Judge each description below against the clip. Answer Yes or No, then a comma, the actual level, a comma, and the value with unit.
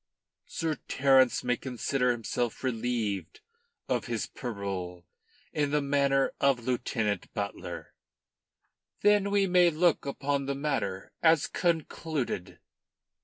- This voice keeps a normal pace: No, slow, 110 wpm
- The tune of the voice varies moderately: Yes, average, 4.7 semitones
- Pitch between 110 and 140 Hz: Yes, low, 135 Hz